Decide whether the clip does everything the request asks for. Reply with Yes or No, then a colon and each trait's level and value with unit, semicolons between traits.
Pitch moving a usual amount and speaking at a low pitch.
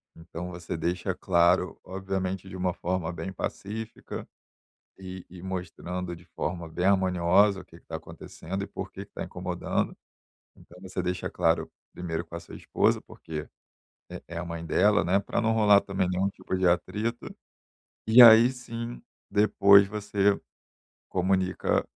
No: narrow, 2.3 semitones; very low, 95 Hz